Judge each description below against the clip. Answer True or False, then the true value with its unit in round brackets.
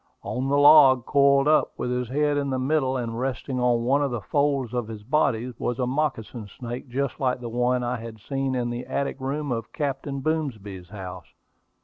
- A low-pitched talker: True (130 Hz)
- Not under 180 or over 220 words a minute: True (205 wpm)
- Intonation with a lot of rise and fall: False (2.6 semitones)